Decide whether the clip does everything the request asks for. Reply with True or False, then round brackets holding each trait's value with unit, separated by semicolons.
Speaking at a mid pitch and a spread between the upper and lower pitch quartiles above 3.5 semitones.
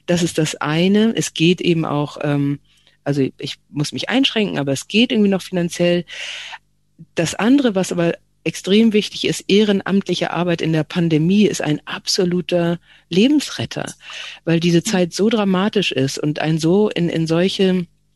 True (175 Hz; 3.9 semitones)